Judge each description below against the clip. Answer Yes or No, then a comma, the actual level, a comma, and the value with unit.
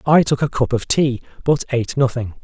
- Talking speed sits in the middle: No, fast, 220 wpm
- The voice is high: No, low, 130 Hz